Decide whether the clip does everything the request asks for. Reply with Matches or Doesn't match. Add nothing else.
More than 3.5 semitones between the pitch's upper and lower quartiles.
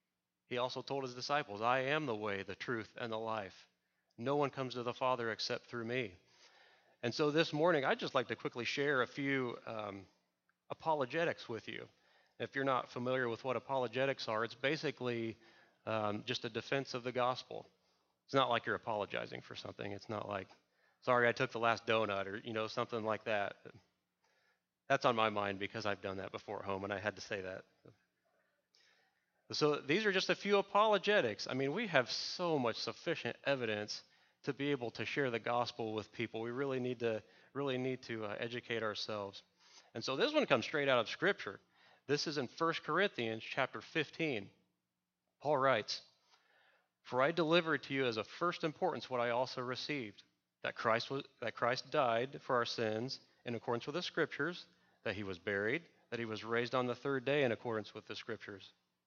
Matches